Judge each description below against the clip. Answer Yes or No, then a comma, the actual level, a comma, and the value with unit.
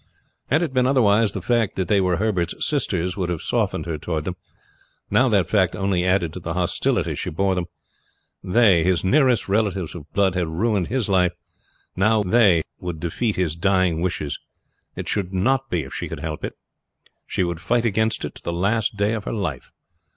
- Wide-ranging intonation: No, average, 4.1 semitones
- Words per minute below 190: No, average, 195 wpm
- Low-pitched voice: Yes, very low, 95 Hz